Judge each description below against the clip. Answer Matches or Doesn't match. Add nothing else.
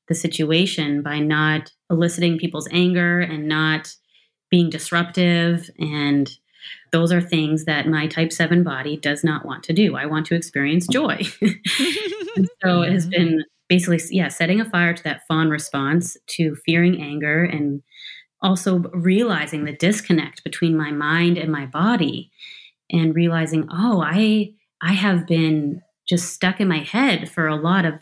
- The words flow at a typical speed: Matches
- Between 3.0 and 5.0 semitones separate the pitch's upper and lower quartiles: Doesn't match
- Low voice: Doesn't match